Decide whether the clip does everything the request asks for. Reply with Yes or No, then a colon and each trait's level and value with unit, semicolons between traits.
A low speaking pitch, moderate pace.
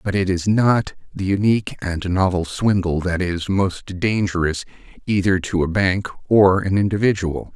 Yes: very low, 95 Hz; average, 160 wpm